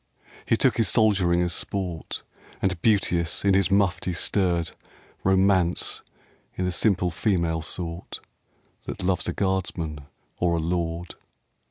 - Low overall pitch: Yes, very low, 90 Hz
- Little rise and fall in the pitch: Yes, narrow, 2.2 semitones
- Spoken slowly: Yes, slow, 130 wpm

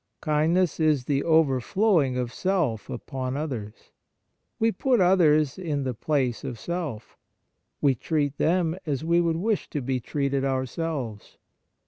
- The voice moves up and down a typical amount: Yes, average, 4.4 semitones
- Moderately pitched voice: Yes, medium, 150 Hz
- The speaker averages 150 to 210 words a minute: No, slow, 135 wpm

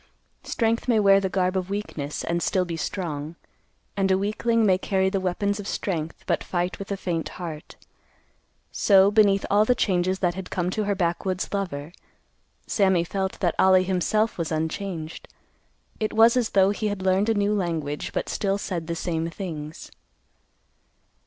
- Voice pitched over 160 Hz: Yes, high, 190 Hz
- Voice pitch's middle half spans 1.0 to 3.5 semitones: Yes, average, 2.8 semitones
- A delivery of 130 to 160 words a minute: No, average, 170 wpm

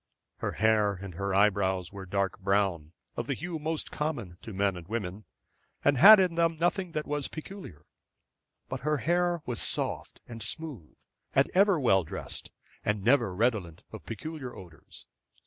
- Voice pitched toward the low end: Yes, low, 115 Hz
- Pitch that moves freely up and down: Yes, wide, 8.4 semitones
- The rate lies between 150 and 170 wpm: Yes, average, 160 wpm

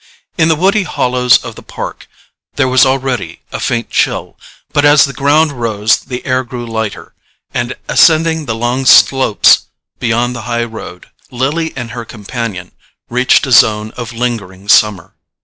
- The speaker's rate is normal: Yes, average, 160 wpm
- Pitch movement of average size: Yes, average, 3.1 semitones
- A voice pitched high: No, low, 125 Hz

